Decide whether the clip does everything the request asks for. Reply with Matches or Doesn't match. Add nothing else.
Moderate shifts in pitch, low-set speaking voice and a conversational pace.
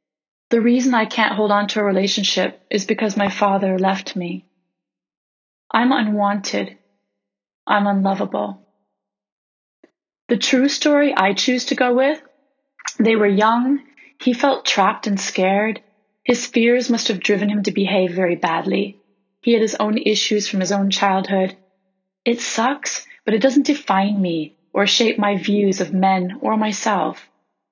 Doesn't match